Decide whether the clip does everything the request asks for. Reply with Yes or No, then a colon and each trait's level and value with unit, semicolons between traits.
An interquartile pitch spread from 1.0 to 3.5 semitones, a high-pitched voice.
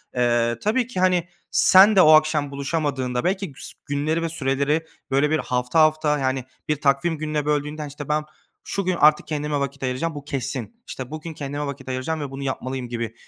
No: average, 2.7 semitones; medium, 145 Hz